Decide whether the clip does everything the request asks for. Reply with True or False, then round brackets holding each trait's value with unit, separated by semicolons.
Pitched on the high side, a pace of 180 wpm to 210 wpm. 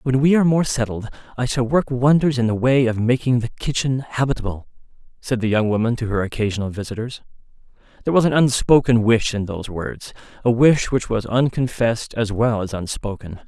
False (120 Hz; 185 wpm)